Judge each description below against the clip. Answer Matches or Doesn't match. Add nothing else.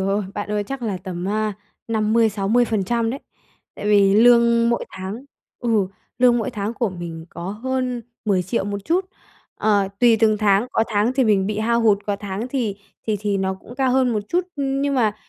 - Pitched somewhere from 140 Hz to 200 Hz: Doesn't match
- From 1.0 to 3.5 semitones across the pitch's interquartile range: Matches